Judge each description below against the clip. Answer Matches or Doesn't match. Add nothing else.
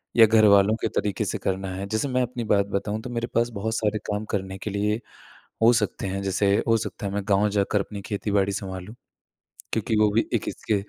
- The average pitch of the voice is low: Matches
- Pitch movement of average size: Doesn't match